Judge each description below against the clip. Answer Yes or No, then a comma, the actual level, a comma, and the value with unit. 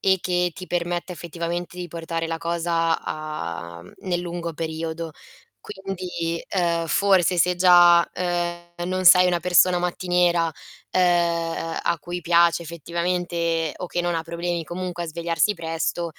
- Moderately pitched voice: Yes, medium, 170 Hz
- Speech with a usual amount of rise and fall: No, narrow, 1.2 semitones